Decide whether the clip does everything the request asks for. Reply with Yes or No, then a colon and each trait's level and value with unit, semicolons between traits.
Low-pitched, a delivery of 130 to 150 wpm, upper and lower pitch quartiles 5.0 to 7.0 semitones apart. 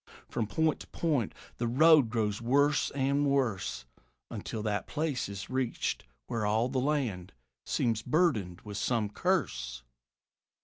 Yes: low, 120 Hz; slow, 135 wpm; wide, 5.4 semitones